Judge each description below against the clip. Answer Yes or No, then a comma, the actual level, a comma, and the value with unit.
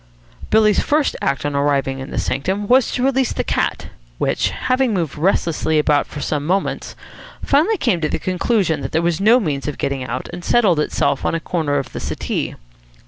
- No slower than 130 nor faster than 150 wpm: No, average, 195 wpm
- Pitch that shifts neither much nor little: No, wide, 7.1 semitones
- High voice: No, medium, 170 Hz